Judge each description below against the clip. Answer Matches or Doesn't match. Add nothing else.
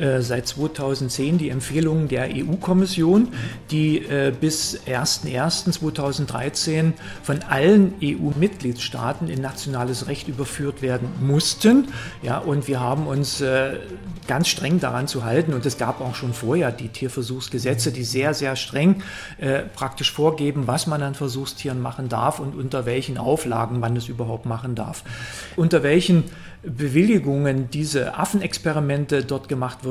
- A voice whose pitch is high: Doesn't match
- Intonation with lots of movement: Doesn't match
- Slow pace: Doesn't match